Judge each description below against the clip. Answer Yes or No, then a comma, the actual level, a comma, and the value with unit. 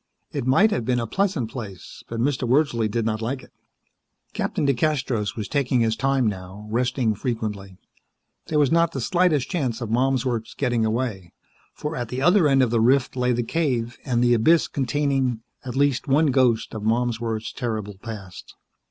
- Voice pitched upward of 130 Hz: No, low, 125 Hz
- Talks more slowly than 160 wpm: No, average, 180 wpm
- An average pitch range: Yes, average, 3.5 semitones